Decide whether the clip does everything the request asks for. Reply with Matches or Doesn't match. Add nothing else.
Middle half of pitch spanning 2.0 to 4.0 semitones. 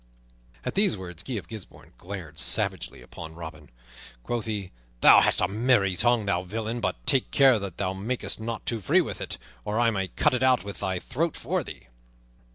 Doesn't match